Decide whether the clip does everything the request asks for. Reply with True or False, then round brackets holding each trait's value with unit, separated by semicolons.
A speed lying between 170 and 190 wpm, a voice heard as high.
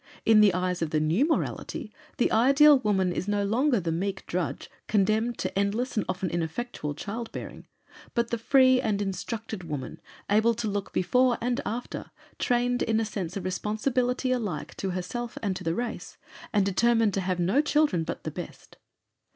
True (180 wpm; 215 Hz)